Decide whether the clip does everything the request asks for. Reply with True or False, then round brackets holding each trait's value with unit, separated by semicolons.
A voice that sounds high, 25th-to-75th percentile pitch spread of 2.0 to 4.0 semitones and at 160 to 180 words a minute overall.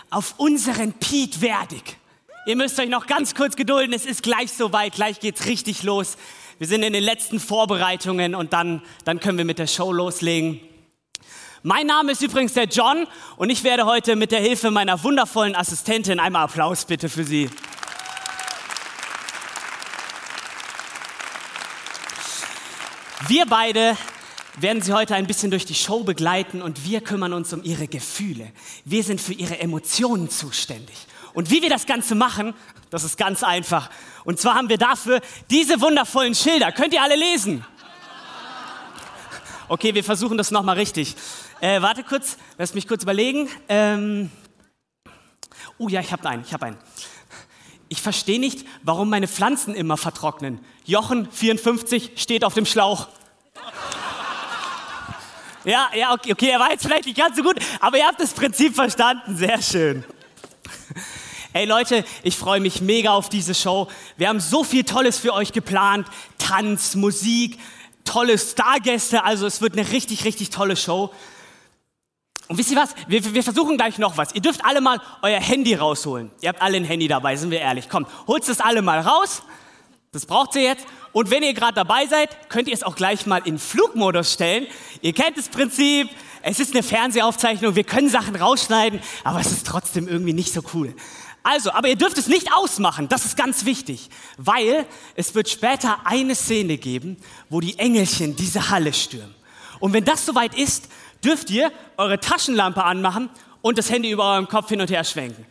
False (215 Hz; 5.4 semitones; 170 wpm)